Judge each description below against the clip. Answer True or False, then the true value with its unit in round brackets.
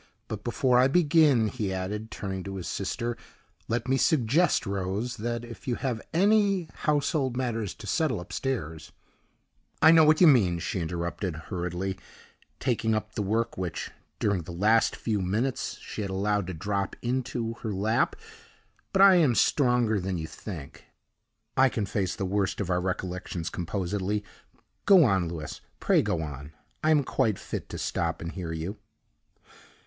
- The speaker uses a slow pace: False (165 wpm)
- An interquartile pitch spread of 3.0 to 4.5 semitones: False (5.5 semitones)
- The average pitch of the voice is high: False (105 Hz)